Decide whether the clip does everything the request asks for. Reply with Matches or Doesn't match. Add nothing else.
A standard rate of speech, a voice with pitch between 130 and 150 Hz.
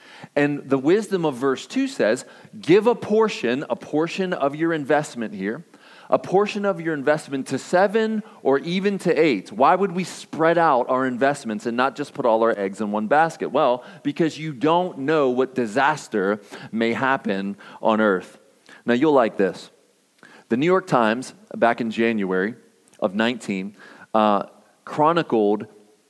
Matches